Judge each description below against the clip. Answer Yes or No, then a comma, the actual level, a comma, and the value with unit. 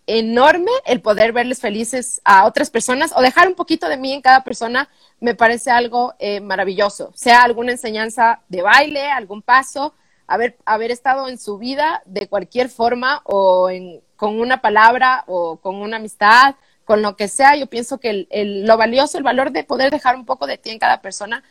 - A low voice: No, high, 240 Hz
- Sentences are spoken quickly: Yes, fast, 195 wpm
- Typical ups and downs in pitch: Yes, average, 3.9 semitones